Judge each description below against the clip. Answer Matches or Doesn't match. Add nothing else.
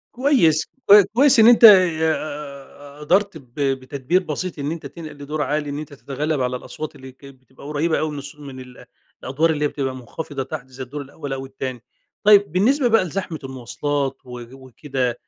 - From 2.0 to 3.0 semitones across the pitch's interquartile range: Doesn't match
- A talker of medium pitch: Matches